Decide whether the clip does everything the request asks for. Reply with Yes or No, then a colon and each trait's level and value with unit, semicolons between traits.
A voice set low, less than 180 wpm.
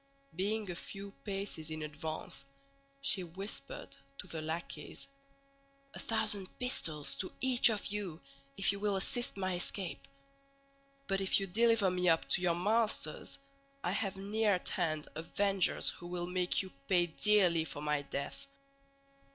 No: high, 190 Hz; average, 150 wpm